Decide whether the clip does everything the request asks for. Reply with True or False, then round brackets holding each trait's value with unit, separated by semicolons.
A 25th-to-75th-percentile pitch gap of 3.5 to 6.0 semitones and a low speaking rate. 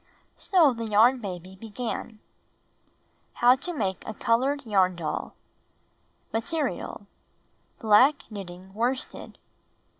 True (4.7 semitones; 95 wpm)